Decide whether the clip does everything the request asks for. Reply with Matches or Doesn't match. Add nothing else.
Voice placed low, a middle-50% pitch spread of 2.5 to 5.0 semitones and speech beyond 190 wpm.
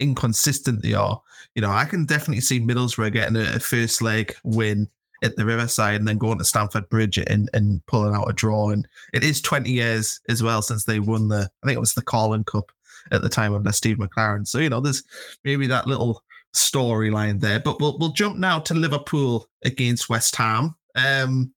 Matches